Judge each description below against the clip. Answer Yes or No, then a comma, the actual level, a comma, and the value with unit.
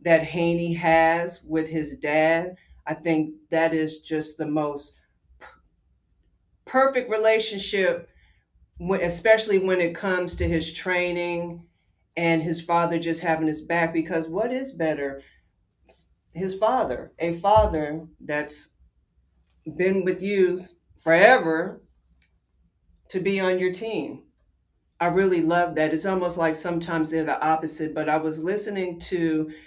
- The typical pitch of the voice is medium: Yes, medium, 165 Hz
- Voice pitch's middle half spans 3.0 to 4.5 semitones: No, narrow, 2.6 semitones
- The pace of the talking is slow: Yes, slow, 130 wpm